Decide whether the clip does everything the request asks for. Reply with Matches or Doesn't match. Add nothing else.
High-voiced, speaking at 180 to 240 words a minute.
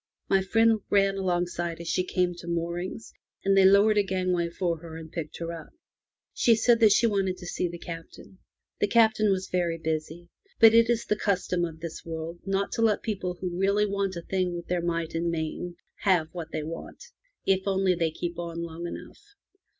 Doesn't match